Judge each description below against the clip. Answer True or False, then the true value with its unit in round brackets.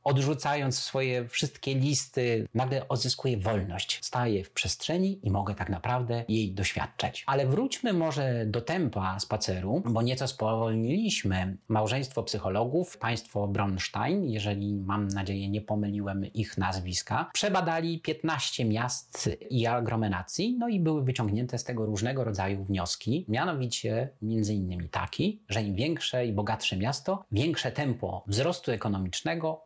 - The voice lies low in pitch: True (115 Hz)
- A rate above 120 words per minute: True (130 wpm)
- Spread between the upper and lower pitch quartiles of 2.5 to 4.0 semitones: False (5.2 semitones)